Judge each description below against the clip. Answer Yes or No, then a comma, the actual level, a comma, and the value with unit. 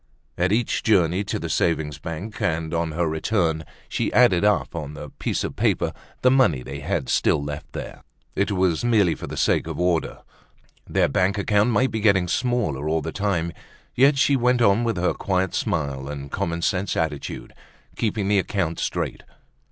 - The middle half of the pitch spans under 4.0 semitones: No, average, 4.9 semitones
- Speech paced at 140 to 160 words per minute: No, average, 185 wpm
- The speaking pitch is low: Yes, very low, 90 Hz